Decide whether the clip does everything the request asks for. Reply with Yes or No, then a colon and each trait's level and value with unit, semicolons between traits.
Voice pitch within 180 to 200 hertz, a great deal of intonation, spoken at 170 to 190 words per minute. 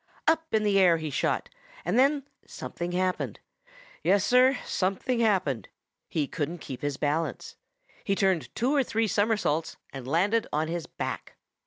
No: medium, 185 Hz; wide, 6.1 semitones; average, 155 wpm